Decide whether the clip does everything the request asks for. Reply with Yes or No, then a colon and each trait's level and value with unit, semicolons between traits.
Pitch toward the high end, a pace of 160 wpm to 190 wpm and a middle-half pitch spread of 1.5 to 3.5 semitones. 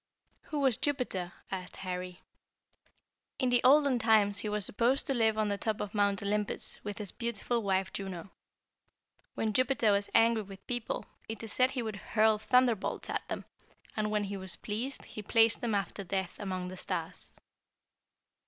Yes: high, 210 Hz; average, 170 wpm; average, 2.9 semitones